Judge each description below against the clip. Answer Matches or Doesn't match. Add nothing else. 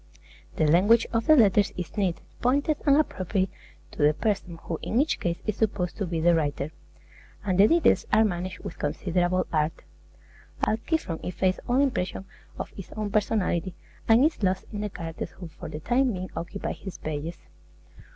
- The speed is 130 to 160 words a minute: Doesn't match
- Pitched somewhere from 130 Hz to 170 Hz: Doesn't match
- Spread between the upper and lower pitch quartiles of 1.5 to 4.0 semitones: Doesn't match